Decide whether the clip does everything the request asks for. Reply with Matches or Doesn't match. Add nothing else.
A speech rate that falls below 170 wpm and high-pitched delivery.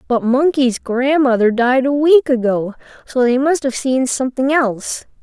Matches